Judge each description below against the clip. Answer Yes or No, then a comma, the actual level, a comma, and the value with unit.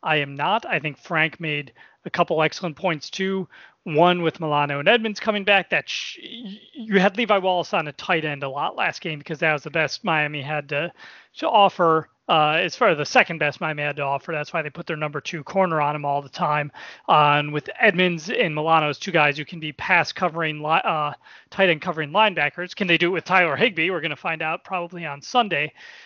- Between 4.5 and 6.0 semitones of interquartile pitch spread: No, average, 3.8 semitones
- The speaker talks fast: Yes, fast, 235 wpm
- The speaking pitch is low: No, medium, 165 Hz